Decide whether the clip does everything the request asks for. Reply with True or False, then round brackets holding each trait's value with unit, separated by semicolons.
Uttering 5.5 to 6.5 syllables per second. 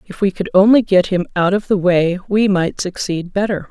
False (5.1 syllables/s)